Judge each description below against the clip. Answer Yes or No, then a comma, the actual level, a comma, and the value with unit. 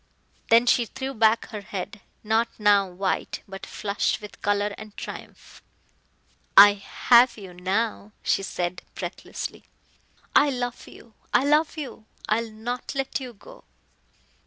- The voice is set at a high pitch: Yes, high, 220 Hz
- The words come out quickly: No, average, 140 wpm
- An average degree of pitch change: Yes, average, 3.3 semitones